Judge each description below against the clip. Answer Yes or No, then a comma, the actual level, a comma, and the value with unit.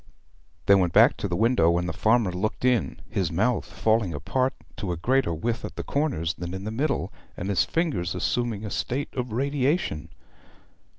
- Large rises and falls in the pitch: Yes, wide, 6.5 semitones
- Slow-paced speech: No, average, 185 wpm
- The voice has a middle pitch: No, low, 110 Hz